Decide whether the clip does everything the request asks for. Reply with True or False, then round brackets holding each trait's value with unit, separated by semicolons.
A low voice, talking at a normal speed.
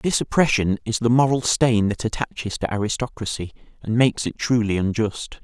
True (115 Hz; 165 wpm)